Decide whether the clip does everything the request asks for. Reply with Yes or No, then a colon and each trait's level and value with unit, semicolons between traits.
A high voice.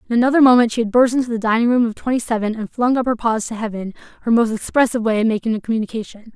Yes: high, 230 Hz